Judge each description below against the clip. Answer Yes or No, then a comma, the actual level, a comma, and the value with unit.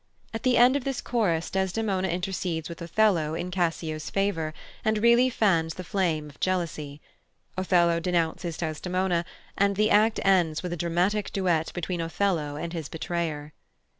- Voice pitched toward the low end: No, medium, 175 Hz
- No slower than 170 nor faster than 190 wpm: No, average, 155 wpm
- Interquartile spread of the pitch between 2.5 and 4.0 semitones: Yes, average, 3.3 semitones